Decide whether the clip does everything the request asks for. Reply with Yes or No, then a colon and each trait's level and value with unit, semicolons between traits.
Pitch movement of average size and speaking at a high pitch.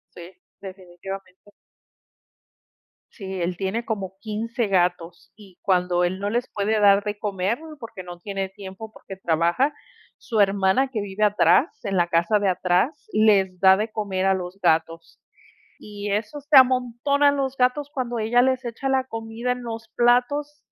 Yes: average, 4.2 semitones; high, 205 Hz